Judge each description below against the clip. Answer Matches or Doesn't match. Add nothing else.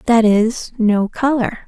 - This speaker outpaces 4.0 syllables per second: Doesn't match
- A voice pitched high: Matches